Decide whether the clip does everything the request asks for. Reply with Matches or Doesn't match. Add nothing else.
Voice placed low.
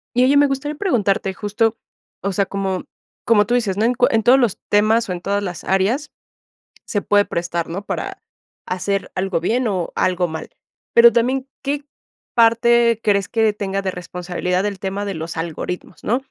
Doesn't match